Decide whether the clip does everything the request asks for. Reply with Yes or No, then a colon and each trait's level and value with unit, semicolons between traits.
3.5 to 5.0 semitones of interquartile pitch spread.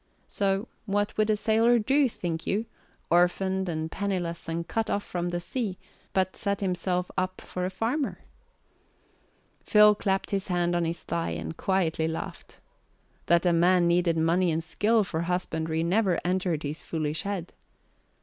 No: average, 3.1 semitones